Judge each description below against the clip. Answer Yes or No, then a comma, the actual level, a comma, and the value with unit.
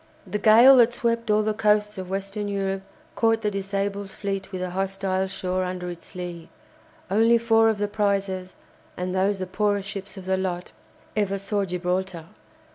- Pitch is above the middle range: Yes, high, 195 Hz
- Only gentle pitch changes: Yes, narrow, 2.0 semitones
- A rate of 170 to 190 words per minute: Yes, average, 175 wpm